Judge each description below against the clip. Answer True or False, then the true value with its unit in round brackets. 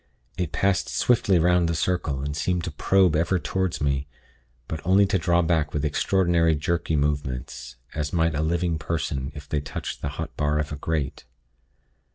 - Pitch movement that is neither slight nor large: True (3.2 semitones)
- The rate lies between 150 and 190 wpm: True (180 wpm)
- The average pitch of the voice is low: True (80 Hz)